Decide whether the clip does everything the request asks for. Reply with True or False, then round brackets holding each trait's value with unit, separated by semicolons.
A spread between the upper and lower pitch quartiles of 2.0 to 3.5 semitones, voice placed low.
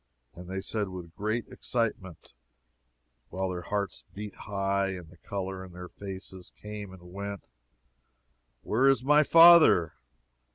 True (2.4 semitones; 95 Hz)